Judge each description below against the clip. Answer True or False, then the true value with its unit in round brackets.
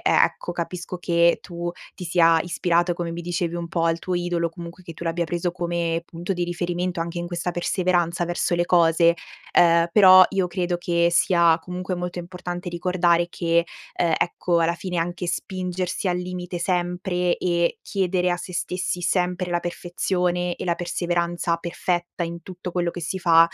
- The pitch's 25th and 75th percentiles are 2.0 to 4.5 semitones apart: False (0.8 semitones)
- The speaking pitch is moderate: True (175 Hz)